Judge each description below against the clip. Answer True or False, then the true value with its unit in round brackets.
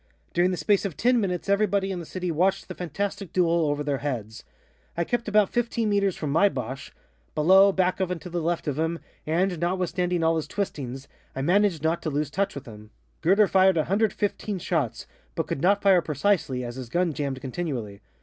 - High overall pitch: False (175 Hz)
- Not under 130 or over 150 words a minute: False (200 wpm)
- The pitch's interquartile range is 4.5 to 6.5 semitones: True (4.9 semitones)